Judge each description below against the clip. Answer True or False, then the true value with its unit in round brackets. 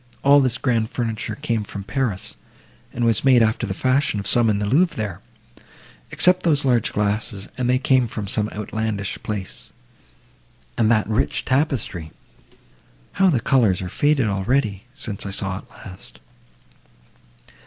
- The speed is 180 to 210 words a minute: False (150 wpm)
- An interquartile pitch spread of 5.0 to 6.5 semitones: False (4.2 semitones)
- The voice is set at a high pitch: False (110 Hz)